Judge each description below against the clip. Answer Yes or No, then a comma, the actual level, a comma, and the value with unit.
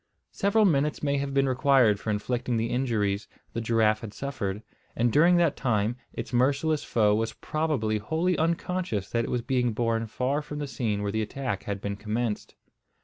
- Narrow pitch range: No, average, 4.7 semitones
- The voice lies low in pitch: Yes, low, 120 Hz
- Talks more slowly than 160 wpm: No, average, 185 wpm